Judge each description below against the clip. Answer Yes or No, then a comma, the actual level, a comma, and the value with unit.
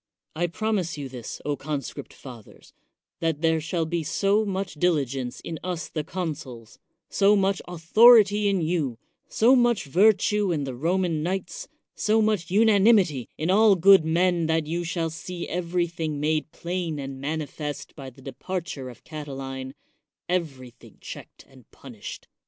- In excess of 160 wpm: No, average, 150 wpm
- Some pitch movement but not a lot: Yes, average, 4.6 semitones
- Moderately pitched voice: Yes, medium, 165 Hz